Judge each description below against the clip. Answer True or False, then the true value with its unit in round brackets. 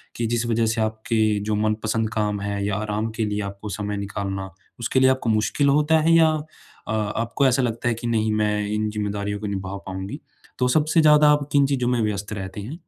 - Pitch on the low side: True (110 Hz)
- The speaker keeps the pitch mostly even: False (3.2 semitones)